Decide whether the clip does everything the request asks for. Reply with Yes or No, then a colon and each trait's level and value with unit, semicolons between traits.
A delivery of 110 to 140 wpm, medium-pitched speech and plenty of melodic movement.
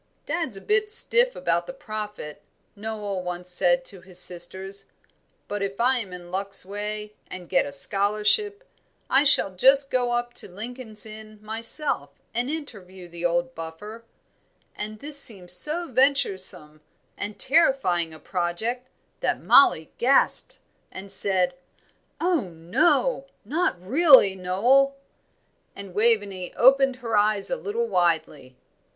No: slow, 135 wpm; high, 210 Hz; wide, 6.5 semitones